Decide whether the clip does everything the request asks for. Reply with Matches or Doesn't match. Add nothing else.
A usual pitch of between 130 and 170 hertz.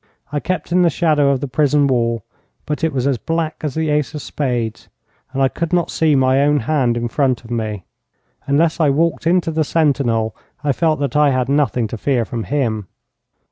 Matches